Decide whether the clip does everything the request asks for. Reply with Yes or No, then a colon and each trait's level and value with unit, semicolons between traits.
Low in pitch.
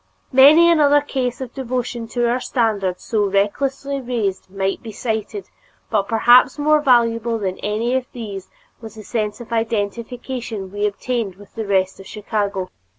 No: high, 230 Hz